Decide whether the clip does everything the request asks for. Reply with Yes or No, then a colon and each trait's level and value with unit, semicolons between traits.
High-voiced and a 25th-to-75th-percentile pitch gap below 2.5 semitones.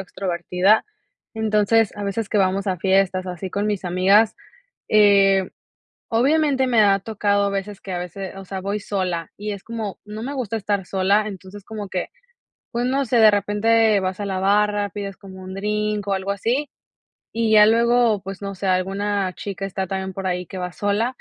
Yes: high, 200 Hz; narrow, 2.0 semitones